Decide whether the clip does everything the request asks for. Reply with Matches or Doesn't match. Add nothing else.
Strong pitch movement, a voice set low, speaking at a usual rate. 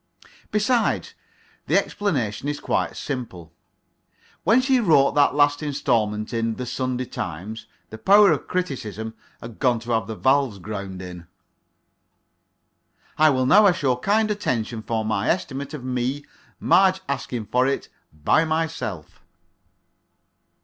Doesn't match